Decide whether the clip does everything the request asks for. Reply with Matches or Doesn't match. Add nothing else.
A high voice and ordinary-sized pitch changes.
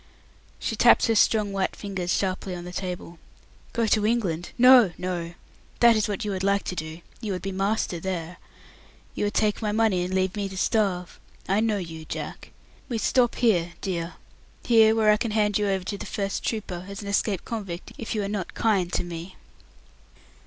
Matches